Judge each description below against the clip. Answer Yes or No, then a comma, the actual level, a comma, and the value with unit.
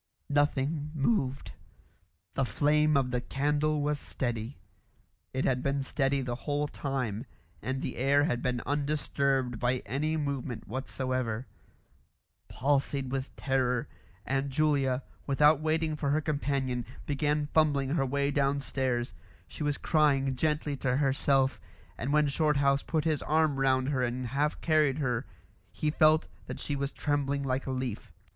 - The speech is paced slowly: No, average, 145 wpm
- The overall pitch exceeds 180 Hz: No, medium, 140 Hz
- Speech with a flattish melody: Yes, narrow, 2.1 semitones